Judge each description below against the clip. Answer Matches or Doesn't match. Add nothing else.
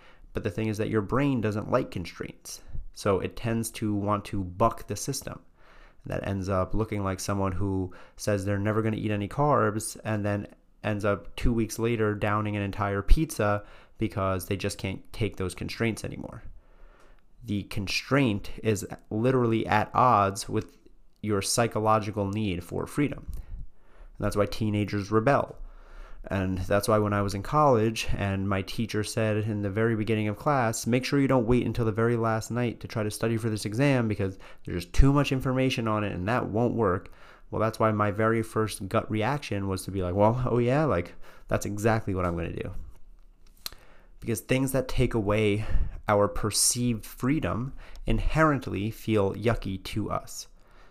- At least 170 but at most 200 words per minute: Matches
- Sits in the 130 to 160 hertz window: Doesn't match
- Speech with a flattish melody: Matches